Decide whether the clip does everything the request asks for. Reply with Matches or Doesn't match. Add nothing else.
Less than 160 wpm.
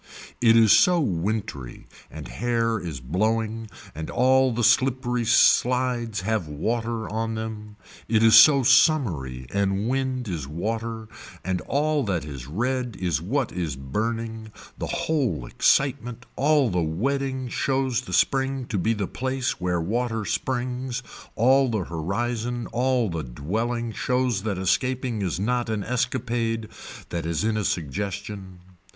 Matches